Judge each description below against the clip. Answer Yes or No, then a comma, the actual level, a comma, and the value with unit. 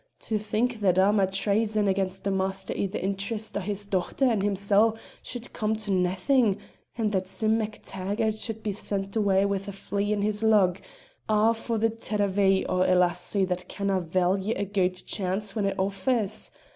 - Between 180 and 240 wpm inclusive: Yes, average, 185 wpm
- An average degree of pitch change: No, narrow, 2.1 semitones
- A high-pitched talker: Yes, high, 200 Hz